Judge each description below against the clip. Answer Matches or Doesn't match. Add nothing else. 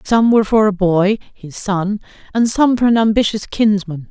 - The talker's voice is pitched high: Matches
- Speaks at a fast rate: Doesn't match